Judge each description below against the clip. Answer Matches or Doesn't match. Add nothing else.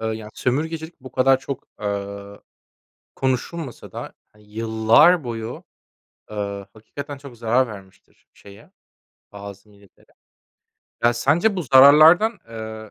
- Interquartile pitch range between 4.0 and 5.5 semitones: Matches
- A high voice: Doesn't match